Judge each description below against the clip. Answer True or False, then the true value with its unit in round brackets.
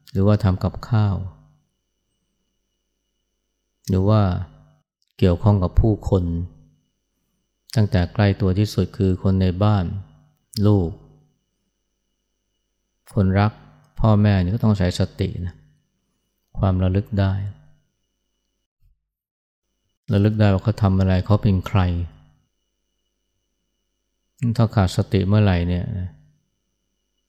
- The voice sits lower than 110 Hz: True (95 Hz)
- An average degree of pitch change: False (2.3 semitones)